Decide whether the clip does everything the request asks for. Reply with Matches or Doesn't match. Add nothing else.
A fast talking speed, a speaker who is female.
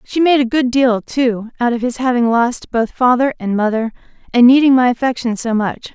Matches